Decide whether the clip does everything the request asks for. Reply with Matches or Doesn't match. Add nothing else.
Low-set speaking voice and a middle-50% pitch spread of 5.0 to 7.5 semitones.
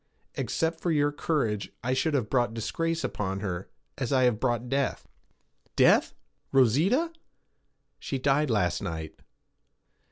Matches